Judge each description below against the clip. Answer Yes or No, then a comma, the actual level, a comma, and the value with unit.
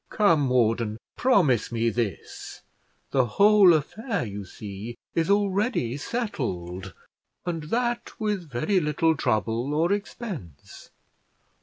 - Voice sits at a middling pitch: Yes, medium, 150 Hz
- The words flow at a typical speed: No, slow, 110 wpm